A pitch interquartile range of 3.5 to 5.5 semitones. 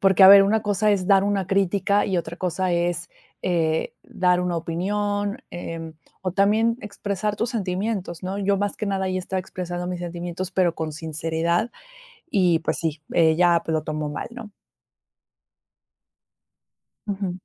No: average, 2.8 semitones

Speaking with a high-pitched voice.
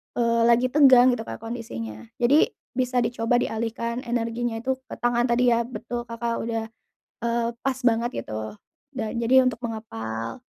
Yes: high, 235 Hz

